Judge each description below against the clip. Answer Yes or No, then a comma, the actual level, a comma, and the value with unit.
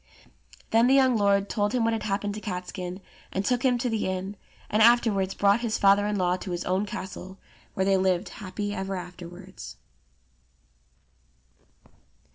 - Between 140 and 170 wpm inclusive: Yes, average, 165 wpm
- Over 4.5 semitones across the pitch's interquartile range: No, average, 2.7 semitones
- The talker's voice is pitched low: No, high, 200 Hz